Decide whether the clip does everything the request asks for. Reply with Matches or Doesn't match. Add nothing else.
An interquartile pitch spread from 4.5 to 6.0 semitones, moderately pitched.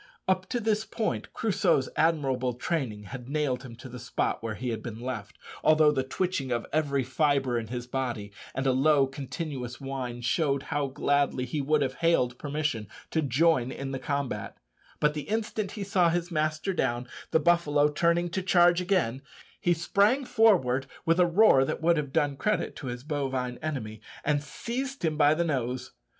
Matches